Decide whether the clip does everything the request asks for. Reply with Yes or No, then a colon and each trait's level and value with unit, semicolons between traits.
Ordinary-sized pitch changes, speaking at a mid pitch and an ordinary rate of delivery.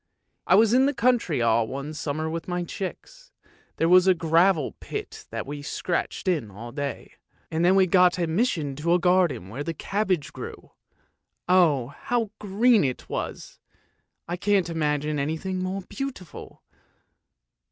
Yes: average, 4.5 semitones; medium, 175 Hz; average, 160 wpm